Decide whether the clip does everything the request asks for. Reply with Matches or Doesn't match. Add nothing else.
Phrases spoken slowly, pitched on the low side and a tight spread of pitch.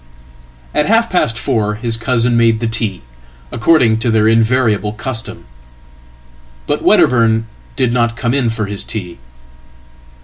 Matches